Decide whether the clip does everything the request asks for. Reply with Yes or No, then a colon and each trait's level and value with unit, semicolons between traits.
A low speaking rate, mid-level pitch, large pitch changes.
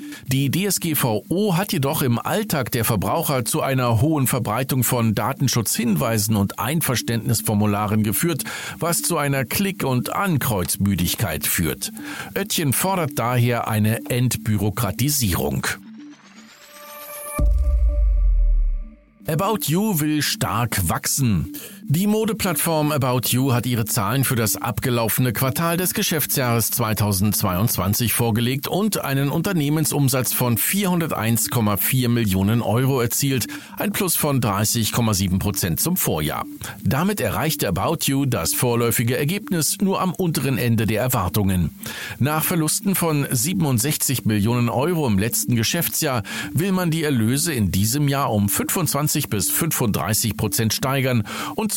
No: slow, 115 wpm; low, 130 Hz; wide, 6.5 semitones